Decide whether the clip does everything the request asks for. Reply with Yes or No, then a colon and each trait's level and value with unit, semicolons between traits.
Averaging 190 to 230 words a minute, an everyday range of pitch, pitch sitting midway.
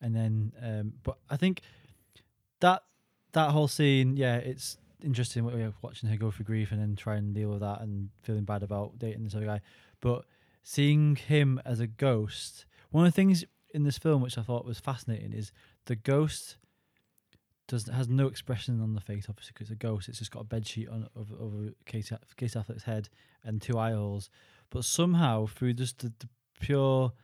No: average, 200 wpm; average, 3.4 semitones; low, 115 Hz